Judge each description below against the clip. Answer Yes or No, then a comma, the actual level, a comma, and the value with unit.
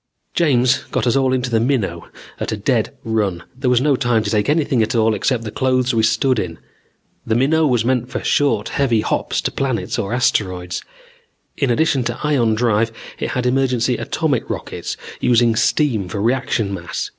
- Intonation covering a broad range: No, average, 3.0 semitones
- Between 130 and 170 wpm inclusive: No, average, 190 wpm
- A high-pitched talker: No, low, 120 Hz